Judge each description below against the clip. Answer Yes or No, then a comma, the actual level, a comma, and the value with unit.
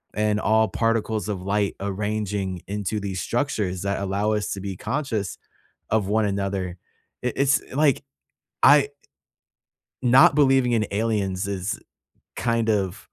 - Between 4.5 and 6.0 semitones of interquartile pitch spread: No, average, 2.7 semitones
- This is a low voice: Yes, low, 105 Hz